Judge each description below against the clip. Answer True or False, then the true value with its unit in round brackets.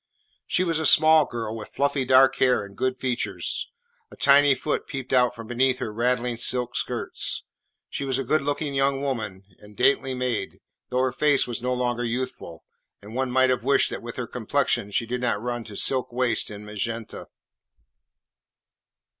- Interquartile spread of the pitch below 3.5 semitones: True (2.5 semitones)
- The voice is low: True (125 Hz)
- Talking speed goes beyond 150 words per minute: True (180 wpm)